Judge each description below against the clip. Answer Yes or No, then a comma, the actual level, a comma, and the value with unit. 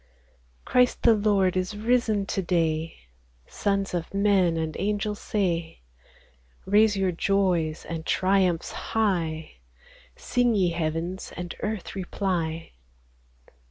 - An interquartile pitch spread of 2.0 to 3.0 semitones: No, average, 3.6 semitones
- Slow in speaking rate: Yes, slow, 110 wpm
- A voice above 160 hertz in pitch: Yes, high, 190 Hz